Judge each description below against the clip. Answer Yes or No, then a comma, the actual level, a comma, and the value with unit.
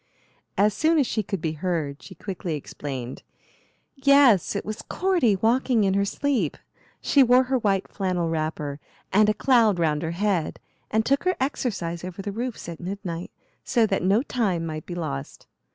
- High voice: Yes, high, 195 Hz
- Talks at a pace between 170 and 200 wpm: Yes, average, 175 wpm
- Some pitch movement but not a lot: No, wide, 6.3 semitones